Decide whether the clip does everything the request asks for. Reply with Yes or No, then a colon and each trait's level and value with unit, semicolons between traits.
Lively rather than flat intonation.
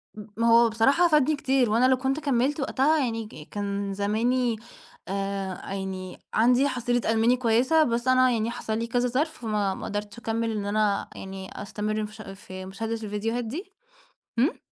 No: average, 3.7 semitones